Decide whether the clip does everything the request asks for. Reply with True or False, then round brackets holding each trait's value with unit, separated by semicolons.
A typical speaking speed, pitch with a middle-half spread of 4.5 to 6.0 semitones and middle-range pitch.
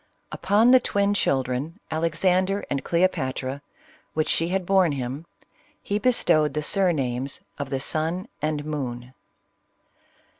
False (120 wpm; 5.6 semitones; 155 Hz)